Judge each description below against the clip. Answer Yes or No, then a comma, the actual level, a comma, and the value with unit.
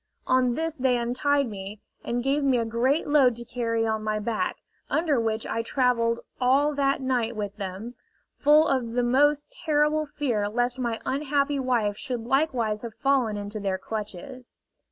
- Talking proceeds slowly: No, average, 170 wpm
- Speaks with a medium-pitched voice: No, high, 245 Hz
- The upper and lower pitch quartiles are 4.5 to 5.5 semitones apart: No, average, 3.7 semitones